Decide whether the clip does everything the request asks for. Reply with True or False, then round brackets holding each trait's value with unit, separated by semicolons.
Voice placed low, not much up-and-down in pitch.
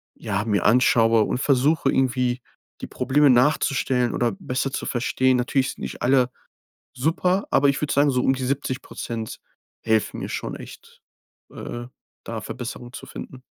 True (125 Hz; 2.1 semitones)